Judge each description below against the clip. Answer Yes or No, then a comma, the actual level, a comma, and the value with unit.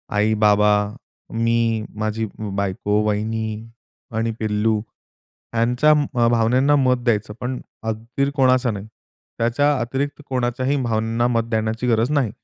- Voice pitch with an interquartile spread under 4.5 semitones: Yes, narrow, 2.6 semitones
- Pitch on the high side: No, low, 115 Hz